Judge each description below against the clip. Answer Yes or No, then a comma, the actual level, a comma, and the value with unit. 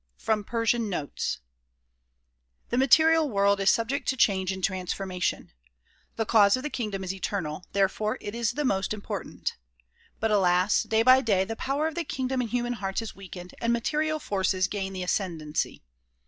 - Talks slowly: No, average, 170 wpm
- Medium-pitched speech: No, high, 210 Hz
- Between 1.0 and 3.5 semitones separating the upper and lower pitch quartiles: No, average, 4.1 semitones